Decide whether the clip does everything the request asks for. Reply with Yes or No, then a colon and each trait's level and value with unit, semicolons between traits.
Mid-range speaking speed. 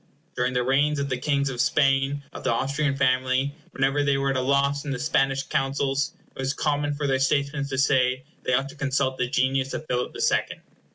No: fast, 225 wpm